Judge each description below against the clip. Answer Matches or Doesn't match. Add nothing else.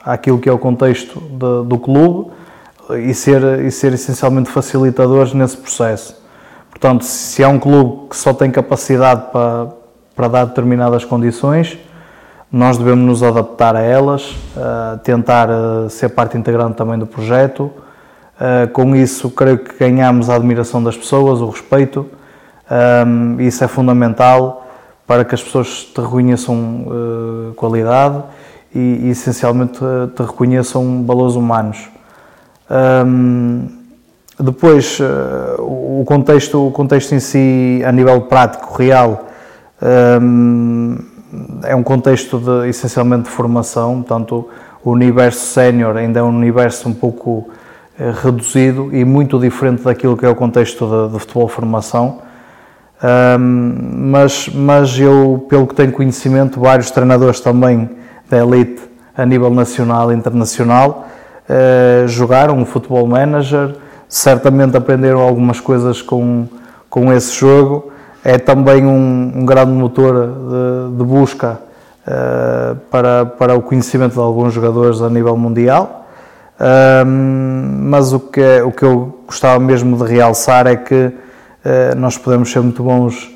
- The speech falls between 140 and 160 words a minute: Doesn't match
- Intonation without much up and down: Matches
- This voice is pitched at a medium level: Doesn't match